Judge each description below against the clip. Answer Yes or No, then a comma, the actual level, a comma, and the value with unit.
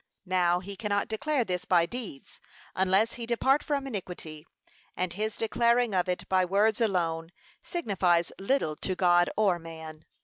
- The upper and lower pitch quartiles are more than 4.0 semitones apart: Yes, average, 4.4 semitones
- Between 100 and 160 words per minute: Yes, average, 150 wpm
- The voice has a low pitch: No, high, 190 Hz